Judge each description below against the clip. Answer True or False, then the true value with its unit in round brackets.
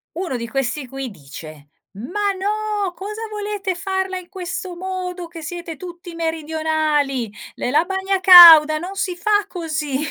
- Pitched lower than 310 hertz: False (345 Hz)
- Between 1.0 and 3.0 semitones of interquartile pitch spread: False (4.1 semitones)